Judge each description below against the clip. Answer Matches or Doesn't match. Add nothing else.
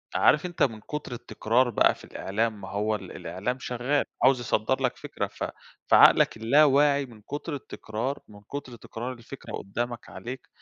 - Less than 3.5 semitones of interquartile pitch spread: Doesn't match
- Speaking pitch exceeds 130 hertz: Doesn't match